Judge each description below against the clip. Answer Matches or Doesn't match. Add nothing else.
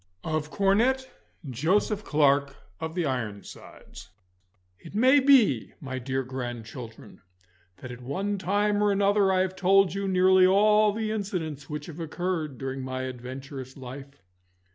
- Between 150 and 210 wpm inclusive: Doesn't match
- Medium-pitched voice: Matches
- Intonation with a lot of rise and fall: Matches